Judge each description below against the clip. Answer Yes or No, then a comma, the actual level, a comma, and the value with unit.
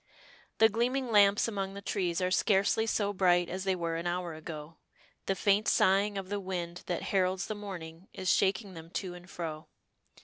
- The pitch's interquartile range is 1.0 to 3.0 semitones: Yes, narrow, 2.5 semitones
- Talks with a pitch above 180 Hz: Yes, high, 190 Hz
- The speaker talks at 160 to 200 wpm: Yes, average, 190 wpm